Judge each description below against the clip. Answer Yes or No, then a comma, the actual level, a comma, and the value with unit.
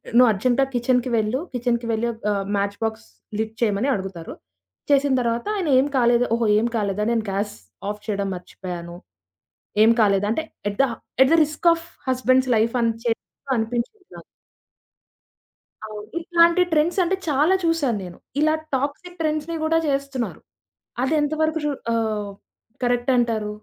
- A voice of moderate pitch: No, high, 240 Hz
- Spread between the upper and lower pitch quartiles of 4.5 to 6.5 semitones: Yes, average, 5.1 semitones